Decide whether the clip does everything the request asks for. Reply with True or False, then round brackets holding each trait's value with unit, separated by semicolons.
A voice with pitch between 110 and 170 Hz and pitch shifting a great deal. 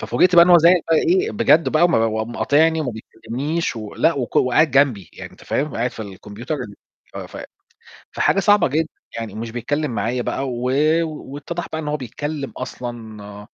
True (135 Hz; 5.8 semitones)